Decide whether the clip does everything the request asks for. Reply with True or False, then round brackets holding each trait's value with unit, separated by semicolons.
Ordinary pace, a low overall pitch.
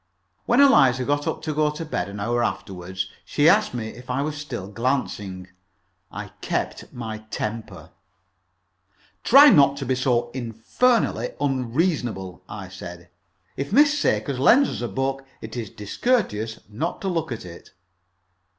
True (150 wpm; 125 Hz)